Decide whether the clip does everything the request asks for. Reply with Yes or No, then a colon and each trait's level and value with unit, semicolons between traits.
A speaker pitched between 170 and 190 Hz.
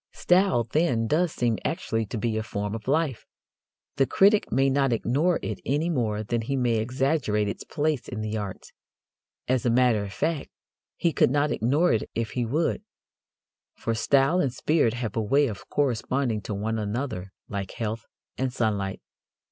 No: low, 120 Hz